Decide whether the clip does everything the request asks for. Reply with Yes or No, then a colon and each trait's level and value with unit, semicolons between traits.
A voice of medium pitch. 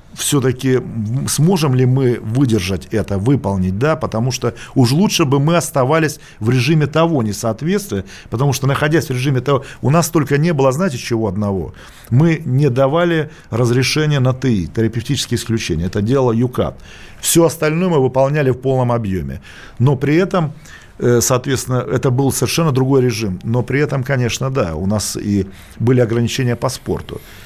No: low, 130 Hz